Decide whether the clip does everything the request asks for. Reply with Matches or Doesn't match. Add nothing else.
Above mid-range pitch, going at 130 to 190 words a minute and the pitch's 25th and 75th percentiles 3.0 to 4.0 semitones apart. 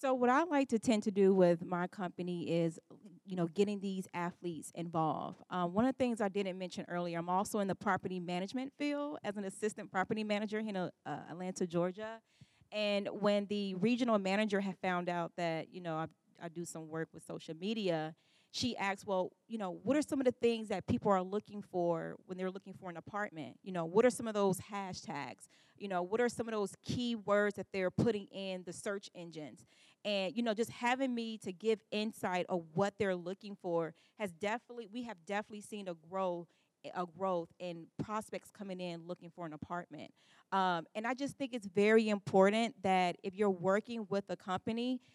Doesn't match